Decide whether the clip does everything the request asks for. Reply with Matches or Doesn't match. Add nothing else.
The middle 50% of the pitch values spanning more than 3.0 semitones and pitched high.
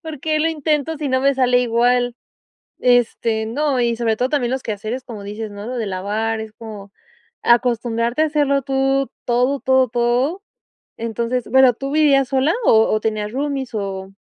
Matches